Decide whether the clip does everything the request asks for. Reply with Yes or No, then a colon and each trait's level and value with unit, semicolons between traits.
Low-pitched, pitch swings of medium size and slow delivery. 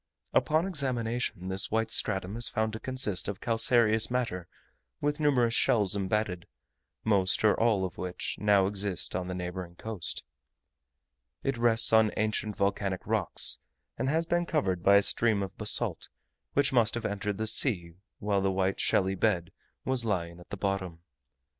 No: low, 105 Hz; average, 3.7 semitones; average, 160 wpm